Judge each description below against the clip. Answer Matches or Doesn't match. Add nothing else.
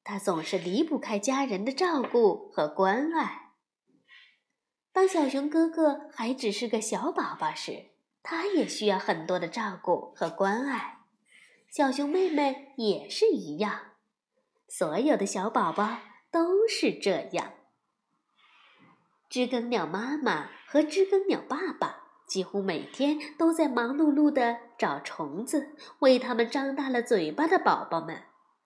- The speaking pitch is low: Doesn't match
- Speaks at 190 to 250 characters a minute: Matches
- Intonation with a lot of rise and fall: Matches